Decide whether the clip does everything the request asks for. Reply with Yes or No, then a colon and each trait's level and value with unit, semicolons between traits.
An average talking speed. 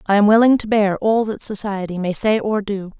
No: fast, 240 wpm